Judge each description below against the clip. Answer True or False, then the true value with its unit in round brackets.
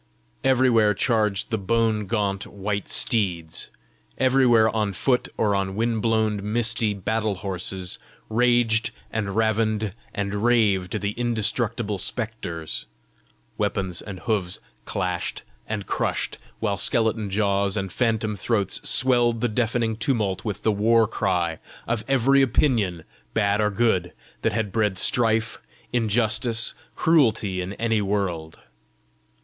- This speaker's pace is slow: True (120 wpm)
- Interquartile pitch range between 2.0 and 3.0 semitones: True (2.7 semitones)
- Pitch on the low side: True (110 Hz)